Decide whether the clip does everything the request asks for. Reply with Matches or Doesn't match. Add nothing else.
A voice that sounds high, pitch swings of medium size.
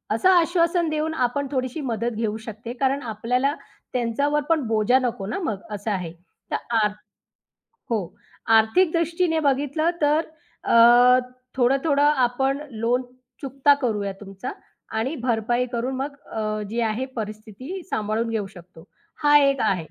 Matches